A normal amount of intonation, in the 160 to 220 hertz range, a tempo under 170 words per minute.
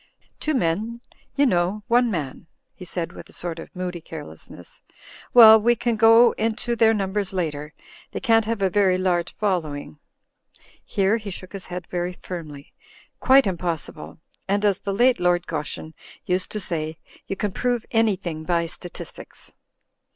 Yes: average, 4.5 semitones; high, 190 Hz; average, 160 wpm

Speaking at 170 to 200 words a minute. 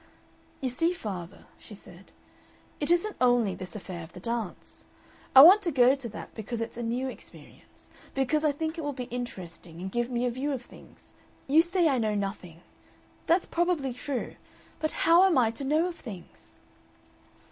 Yes: average, 185 wpm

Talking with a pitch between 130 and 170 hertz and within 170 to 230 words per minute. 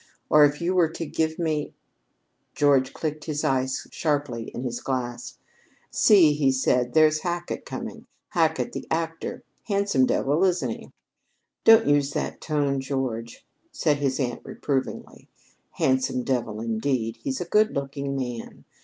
No: medium, 140 Hz; average, 150 wpm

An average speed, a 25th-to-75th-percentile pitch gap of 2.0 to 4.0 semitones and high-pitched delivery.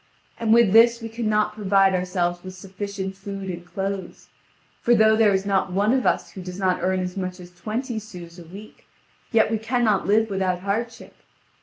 Yes: average, 190 wpm; average, 2.9 semitones; high, 195 Hz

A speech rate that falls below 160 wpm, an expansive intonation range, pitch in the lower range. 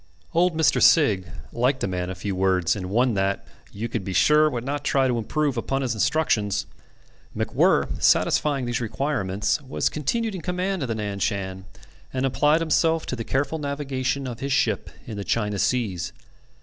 No: average, 180 wpm; wide, 6.2 semitones; low, 125 Hz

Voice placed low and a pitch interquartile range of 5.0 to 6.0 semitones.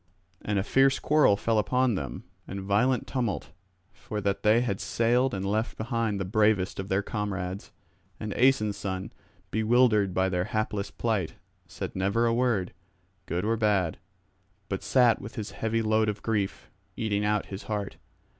No: low, 105 Hz; average, 2.7 semitones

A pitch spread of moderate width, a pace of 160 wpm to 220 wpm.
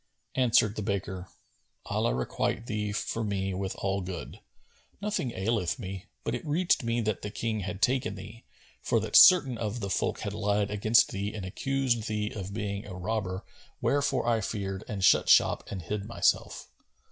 Yes: average, 3.1 semitones; average, 175 wpm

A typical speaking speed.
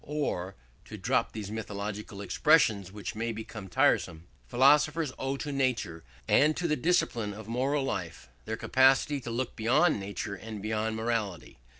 Yes: average, 155 wpm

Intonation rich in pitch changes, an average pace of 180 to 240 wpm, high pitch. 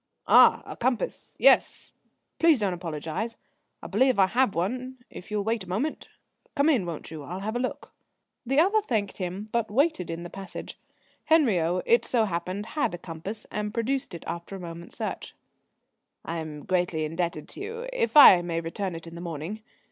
Yes: wide, 6.6 semitones; average, 185 wpm; high, 195 Hz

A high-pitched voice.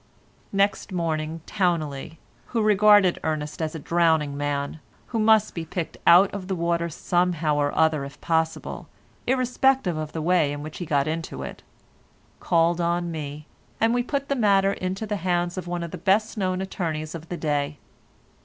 No: medium, 170 Hz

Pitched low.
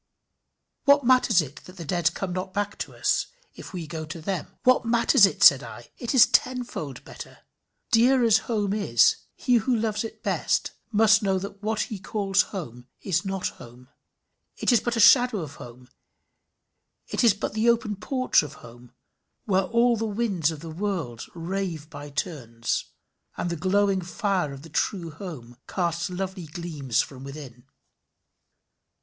No: high, 190 Hz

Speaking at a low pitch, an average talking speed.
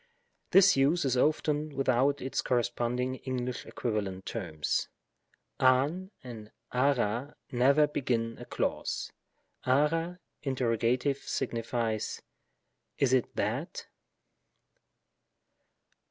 No: low, 130 Hz; slow, 95 wpm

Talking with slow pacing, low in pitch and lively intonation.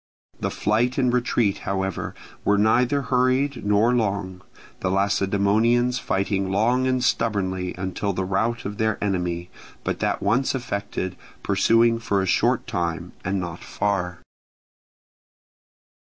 No: slow, 125 wpm; low, 100 Hz; average, 3.7 semitones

